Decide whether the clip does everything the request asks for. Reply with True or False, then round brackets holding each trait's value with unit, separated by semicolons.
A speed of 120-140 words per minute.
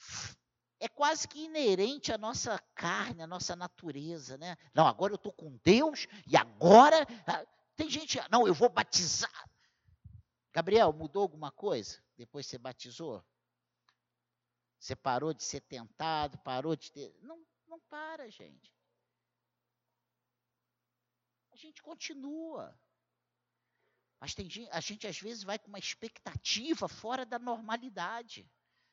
True (125 wpm)